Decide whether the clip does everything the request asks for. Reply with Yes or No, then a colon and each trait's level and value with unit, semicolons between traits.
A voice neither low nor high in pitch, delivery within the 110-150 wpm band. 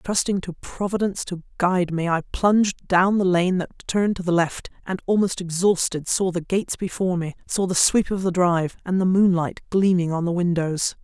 No: medium, 180 Hz; average, 195 wpm